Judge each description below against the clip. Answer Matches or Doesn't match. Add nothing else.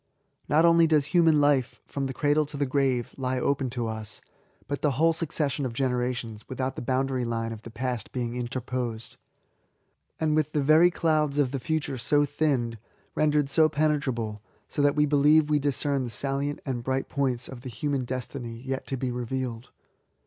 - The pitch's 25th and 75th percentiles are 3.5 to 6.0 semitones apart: Doesn't match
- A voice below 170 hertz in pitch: Matches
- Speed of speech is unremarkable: Matches